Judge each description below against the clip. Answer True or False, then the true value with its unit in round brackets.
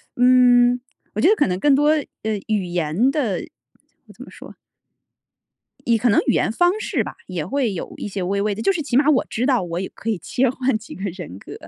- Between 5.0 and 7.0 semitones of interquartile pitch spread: True (5.4 semitones)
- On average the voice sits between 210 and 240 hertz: True (225 Hz)